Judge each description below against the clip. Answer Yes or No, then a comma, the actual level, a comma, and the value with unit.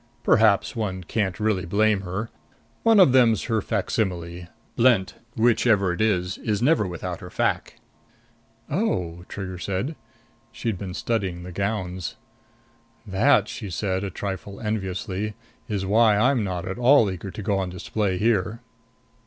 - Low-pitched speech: Yes, low, 100 Hz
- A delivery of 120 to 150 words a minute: Yes, average, 145 wpm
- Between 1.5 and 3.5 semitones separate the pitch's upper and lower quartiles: Yes, average, 3.1 semitones